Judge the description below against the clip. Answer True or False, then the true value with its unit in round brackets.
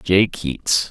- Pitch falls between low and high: False (100 Hz)